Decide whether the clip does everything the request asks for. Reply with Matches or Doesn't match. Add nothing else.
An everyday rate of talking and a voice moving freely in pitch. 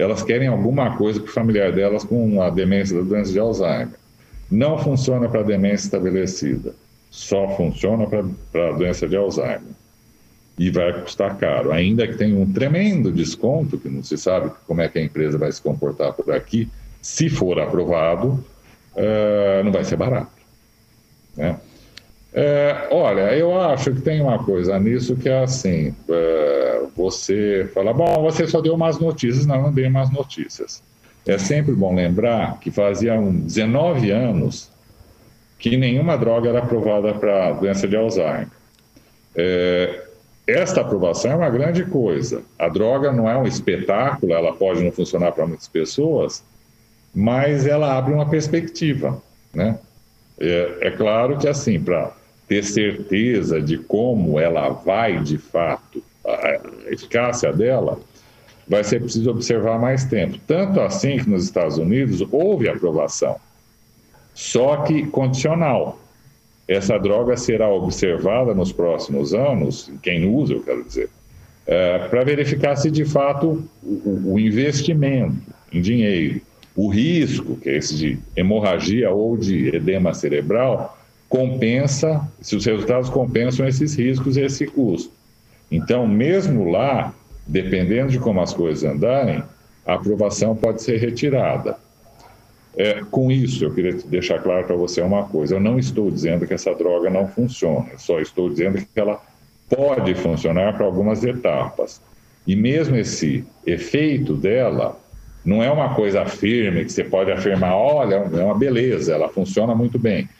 Matches